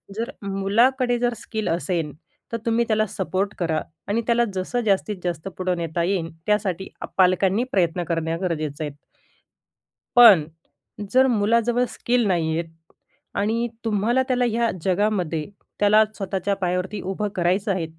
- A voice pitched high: Yes, high, 195 Hz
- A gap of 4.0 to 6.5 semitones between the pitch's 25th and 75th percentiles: Yes, average, 4.3 semitones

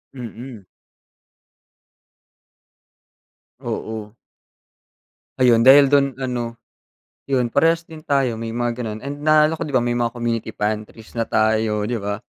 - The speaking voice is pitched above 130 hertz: No, low, 120 Hz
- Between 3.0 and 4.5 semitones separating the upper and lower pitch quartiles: Yes, average, 3.7 semitones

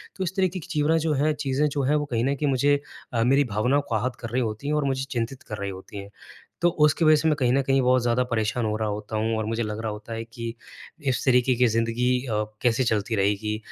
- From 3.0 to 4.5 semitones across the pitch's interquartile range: Yes, average, 4.0 semitones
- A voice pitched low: Yes, low, 125 Hz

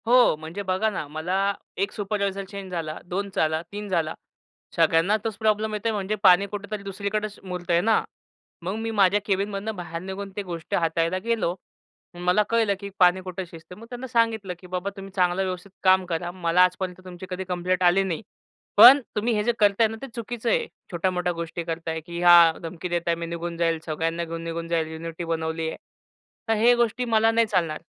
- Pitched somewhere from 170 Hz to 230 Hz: Yes, medium, 185 Hz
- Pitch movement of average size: Yes, average, 3.5 semitones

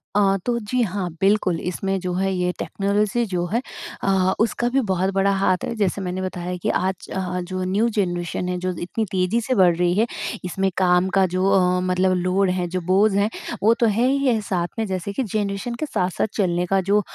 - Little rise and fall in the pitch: Yes, narrow, 2.3 semitones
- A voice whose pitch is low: No, high, 190 Hz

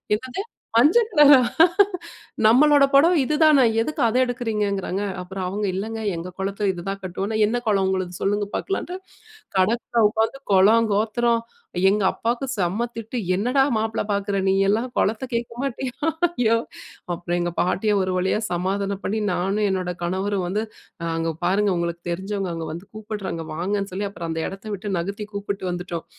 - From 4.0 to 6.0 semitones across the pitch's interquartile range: No, average, 3.6 semitones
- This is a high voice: Yes, high, 205 Hz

